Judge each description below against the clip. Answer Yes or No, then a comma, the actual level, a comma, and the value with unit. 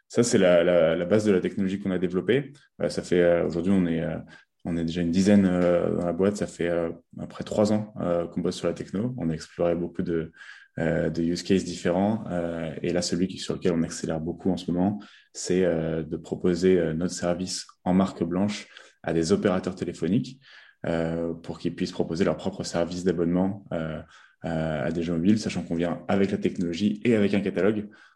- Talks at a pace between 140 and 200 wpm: No, average, 215 wpm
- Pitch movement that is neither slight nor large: No, narrow, 2.1 semitones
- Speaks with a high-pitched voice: No, very low, 85 Hz